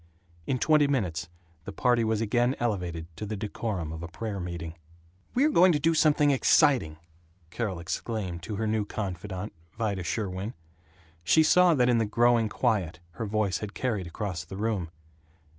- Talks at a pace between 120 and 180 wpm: Yes, average, 165 wpm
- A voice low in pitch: Yes, low, 105 Hz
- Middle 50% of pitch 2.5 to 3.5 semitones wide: No, average, 5.0 semitones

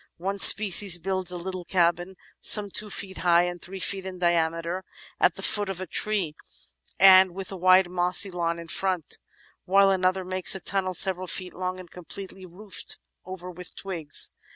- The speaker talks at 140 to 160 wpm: No, average, 175 wpm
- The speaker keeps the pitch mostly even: Yes, narrow, 1.5 semitones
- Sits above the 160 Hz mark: Yes, medium, 185 Hz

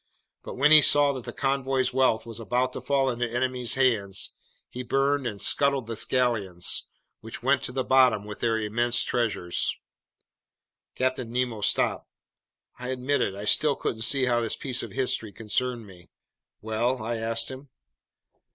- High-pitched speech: No, low, 125 Hz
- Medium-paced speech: Yes, average, 165 wpm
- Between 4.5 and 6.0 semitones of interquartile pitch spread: No, average, 2.8 semitones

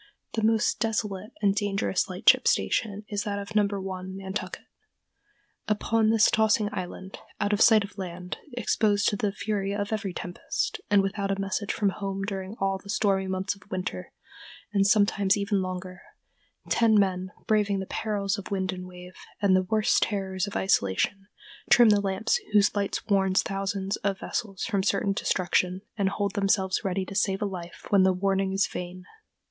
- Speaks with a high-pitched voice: Yes, high, 195 Hz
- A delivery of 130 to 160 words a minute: No, average, 175 wpm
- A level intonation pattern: Yes, narrow, 1.4 semitones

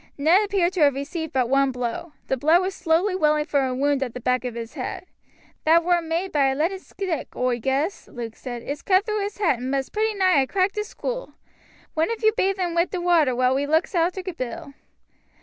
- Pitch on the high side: Yes, very high, 320 Hz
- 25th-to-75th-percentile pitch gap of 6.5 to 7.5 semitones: No, wide, 5.8 semitones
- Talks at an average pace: No, fast, 230 wpm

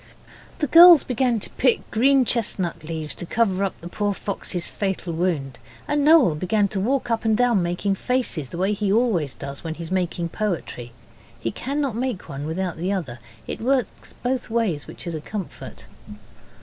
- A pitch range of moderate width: No, wide, 6.2 semitones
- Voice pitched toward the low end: No, high, 195 Hz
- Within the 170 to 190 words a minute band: Yes, average, 180 wpm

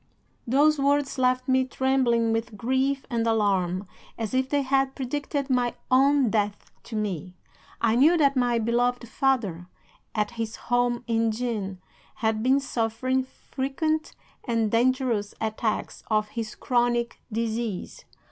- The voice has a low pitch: No, high, 240 Hz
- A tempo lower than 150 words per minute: Yes, slow, 135 wpm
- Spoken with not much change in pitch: No, average, 3.0 semitones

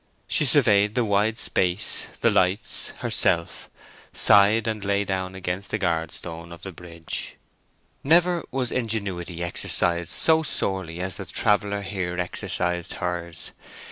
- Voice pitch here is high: No, very low, 95 Hz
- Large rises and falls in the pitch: No, average, 3.2 semitones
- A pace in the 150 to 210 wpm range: No, slow, 135 wpm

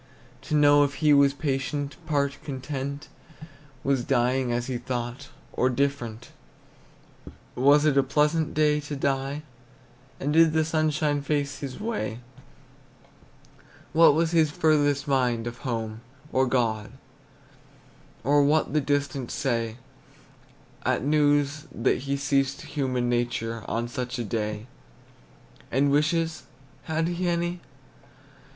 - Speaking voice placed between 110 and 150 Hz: Yes, medium, 140 Hz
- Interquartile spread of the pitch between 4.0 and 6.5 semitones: No, average, 3.1 semitones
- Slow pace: Yes, slow, 125 wpm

